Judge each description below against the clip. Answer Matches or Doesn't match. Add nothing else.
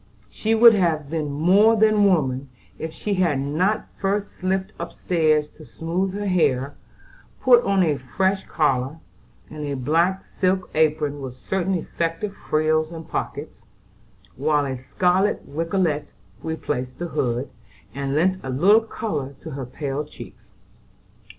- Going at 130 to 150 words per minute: Matches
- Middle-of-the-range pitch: Matches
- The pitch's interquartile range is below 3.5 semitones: Doesn't match